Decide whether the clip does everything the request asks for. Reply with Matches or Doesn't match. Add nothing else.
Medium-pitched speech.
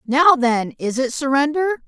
Doesn't match